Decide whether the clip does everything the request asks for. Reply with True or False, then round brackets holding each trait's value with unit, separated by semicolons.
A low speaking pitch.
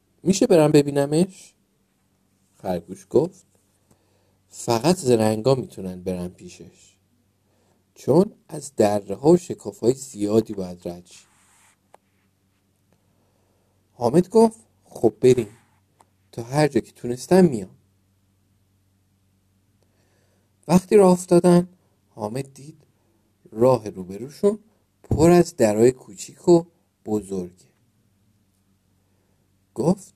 True (105 Hz)